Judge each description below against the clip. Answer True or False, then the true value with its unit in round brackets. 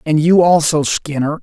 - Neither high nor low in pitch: True (155 Hz)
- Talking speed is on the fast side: False (170 wpm)